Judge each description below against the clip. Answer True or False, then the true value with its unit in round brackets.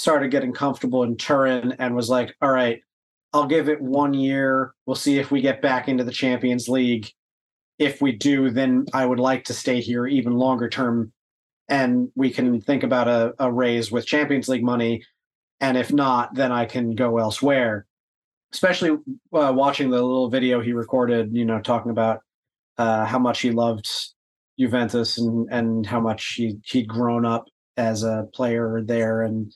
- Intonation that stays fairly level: True (2.2 semitones)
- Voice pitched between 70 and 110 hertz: False (125 Hz)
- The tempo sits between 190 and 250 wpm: False (180 wpm)